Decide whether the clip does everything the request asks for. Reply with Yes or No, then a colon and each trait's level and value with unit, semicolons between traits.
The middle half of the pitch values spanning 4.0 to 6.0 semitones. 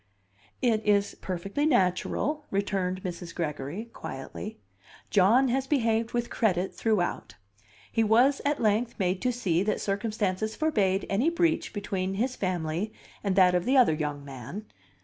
Yes: average, 4.5 semitones